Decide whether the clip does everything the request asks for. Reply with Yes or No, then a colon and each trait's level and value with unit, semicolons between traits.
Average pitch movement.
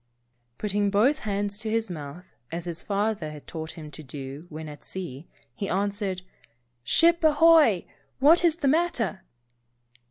No: wide, 6.3 semitones